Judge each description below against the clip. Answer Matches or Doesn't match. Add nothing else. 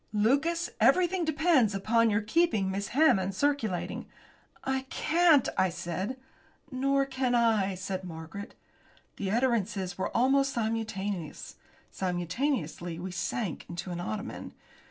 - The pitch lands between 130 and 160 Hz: Doesn't match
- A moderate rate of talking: Doesn't match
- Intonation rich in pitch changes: Matches